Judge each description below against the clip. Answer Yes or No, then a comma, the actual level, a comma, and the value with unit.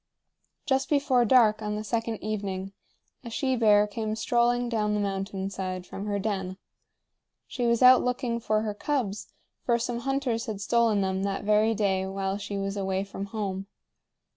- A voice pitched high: Yes, high, 210 Hz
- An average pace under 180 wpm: Yes, average, 170 wpm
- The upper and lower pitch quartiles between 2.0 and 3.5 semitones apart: Yes, average, 3.1 semitones